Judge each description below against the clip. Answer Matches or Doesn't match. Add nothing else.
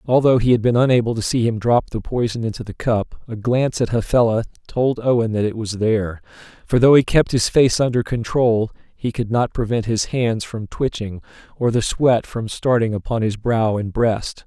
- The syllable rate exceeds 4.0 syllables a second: Matches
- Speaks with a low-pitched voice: Matches